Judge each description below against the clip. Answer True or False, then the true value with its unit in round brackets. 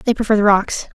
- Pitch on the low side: False (210 Hz)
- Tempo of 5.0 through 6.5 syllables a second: True (5.8 syllables/s)